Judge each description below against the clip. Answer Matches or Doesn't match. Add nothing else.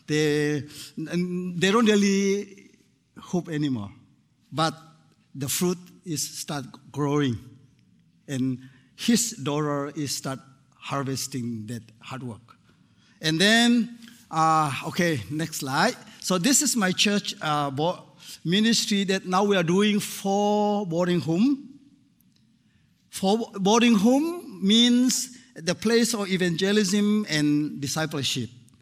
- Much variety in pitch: Matches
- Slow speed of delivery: Matches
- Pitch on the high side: Doesn't match